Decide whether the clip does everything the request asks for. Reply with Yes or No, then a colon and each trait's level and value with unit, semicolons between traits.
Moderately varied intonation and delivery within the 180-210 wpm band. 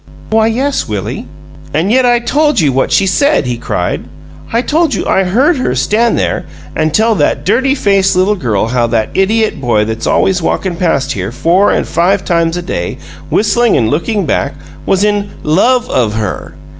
No: wide, 9.0 semitones; average, 185 wpm